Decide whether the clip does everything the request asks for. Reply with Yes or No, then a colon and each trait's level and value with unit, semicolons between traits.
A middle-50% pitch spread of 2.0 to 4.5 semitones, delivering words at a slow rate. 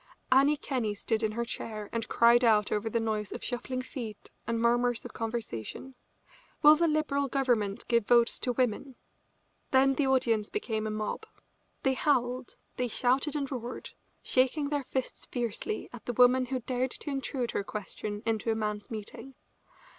No: average, 3.2 semitones; average, 170 wpm